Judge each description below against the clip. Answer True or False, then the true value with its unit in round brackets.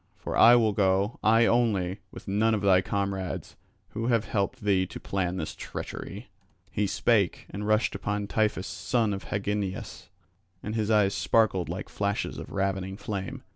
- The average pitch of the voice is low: True (100 Hz)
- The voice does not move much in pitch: True (2.1 semitones)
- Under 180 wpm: True (165 wpm)